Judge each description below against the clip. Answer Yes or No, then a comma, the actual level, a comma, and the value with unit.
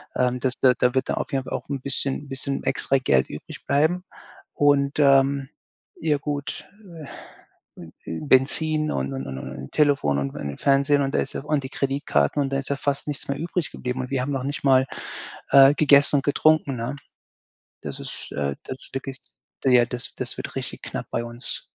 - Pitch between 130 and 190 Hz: Yes, low, 135 Hz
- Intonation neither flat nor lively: No, narrow, 2.3 semitones